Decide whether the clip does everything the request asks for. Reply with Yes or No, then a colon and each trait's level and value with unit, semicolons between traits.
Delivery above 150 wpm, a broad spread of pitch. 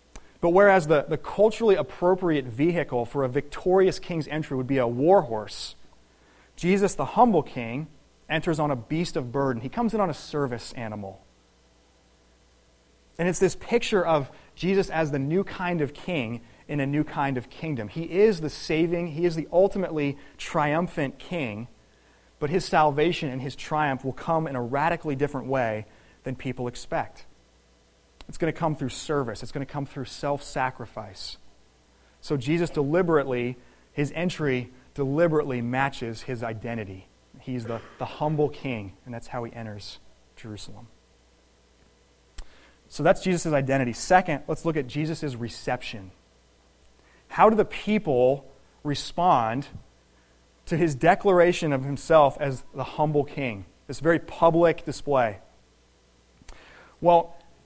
No: average, 145 wpm; wide, 6.8 semitones